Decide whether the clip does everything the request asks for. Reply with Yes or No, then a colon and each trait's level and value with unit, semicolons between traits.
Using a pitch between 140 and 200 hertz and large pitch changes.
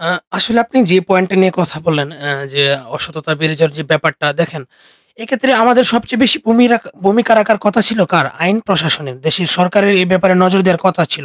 Yes: medium, 185 Hz; wide, 5.8 semitones